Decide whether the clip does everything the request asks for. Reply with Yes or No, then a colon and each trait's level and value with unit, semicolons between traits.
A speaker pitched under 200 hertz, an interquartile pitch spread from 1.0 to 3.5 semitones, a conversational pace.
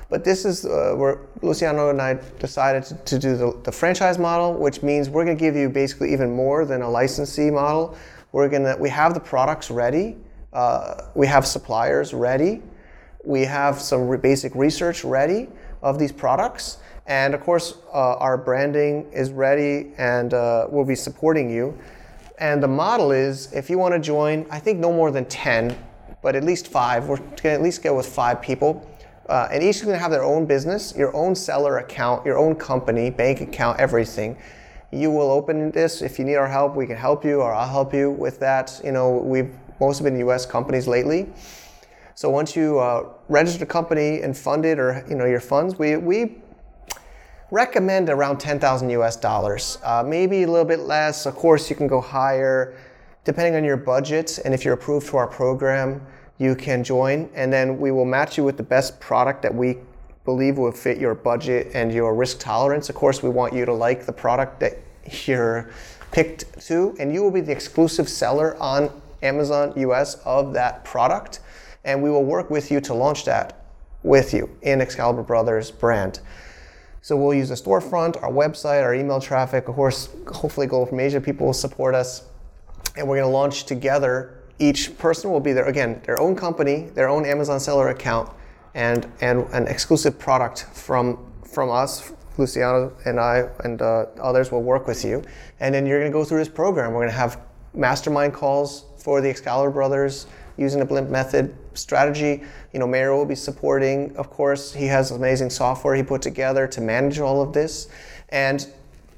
Yes: low, 135 Hz; narrow, 2.5 semitones; average, 195 wpm